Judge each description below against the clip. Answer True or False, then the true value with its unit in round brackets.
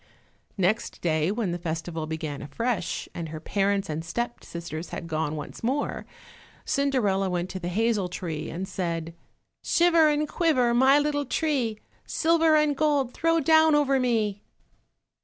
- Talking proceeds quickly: False (155 wpm)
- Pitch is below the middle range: False (210 Hz)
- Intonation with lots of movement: True (9.0 semitones)